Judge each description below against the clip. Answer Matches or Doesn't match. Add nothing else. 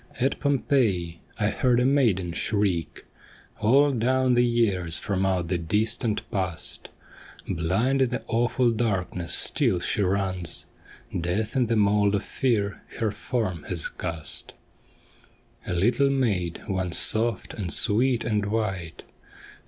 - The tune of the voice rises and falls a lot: Doesn't match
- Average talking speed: Doesn't match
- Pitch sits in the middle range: Doesn't match